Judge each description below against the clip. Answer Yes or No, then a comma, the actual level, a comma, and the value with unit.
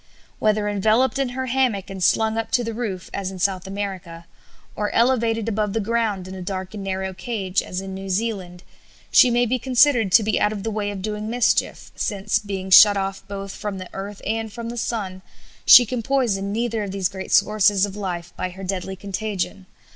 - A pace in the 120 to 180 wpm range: No, fast, 205 wpm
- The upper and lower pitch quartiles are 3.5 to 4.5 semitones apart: No, average, 2.9 semitones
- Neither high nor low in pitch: No, high, 205 Hz